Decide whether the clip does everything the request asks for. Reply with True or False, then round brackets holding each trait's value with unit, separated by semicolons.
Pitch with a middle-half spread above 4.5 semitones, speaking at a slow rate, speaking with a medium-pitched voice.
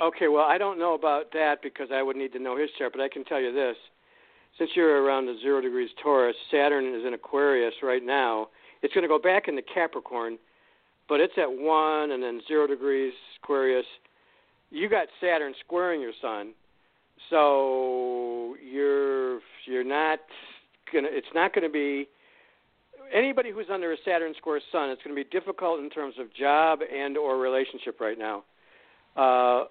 False (5.1 semitones; 180 wpm; 145 Hz)